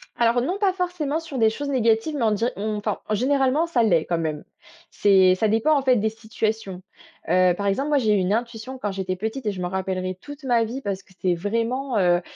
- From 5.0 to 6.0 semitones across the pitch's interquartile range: Yes, wide, 5.5 semitones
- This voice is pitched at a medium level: No, high, 220 Hz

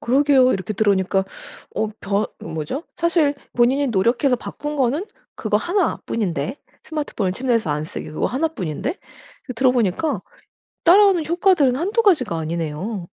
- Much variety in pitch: Yes, wide, 8.1 semitones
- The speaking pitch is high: Yes, very high, 250 Hz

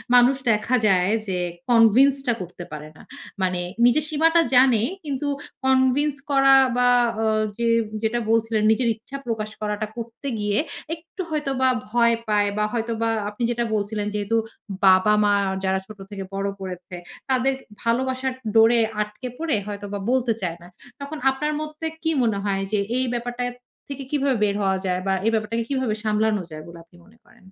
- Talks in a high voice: Yes, high, 230 Hz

